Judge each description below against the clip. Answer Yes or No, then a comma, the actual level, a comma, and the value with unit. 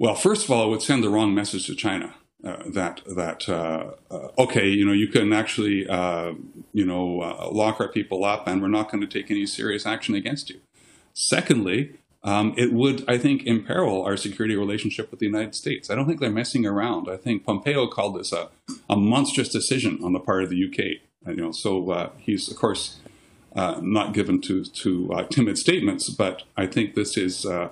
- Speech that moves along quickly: Yes, fast, 215 wpm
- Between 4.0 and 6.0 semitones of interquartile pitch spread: No, average, 3.4 semitones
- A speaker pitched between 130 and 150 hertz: No, low, 105 Hz